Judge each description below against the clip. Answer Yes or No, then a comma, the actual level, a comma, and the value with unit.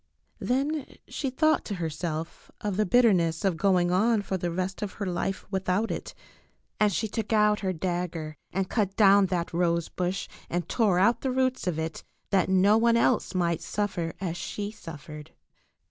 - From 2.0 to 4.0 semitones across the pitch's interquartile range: Yes, average, 3.5 semitones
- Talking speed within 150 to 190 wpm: Yes, average, 180 wpm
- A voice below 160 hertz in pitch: No, high, 190 Hz